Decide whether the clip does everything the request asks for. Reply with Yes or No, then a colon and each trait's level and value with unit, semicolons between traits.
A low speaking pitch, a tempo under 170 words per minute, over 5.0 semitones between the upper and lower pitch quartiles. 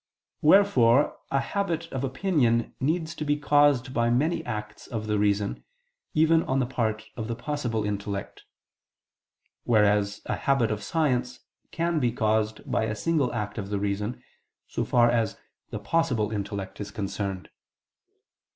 Yes: low, 120 Hz; average, 150 wpm; wide, 5.6 semitones